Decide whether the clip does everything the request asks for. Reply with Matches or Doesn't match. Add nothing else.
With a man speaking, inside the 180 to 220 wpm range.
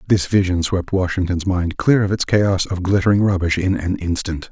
Matches